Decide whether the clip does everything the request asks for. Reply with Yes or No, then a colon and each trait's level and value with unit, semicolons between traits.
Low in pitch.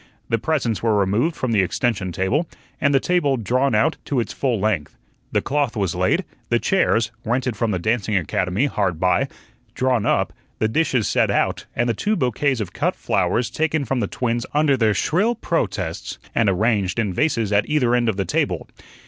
Yes: low, 115 Hz